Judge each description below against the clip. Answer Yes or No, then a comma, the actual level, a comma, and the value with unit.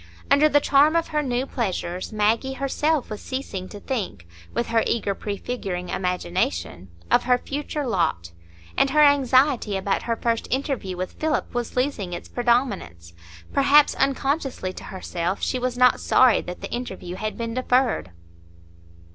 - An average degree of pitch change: No, wide, 6.3 semitones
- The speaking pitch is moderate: No, high, 240 Hz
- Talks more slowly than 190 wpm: Yes, average, 155 wpm